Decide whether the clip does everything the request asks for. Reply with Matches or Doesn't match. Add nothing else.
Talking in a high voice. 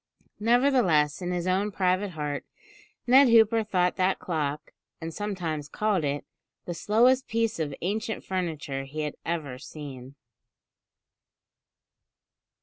Doesn't match